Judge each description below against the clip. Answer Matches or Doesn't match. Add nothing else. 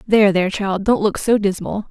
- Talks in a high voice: Matches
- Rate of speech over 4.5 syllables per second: Matches